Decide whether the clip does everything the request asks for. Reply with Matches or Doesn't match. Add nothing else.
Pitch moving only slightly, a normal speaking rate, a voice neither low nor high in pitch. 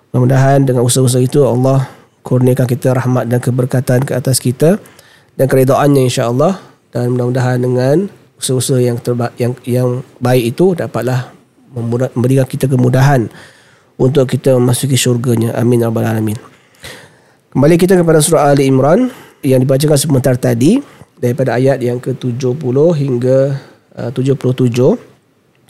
Doesn't match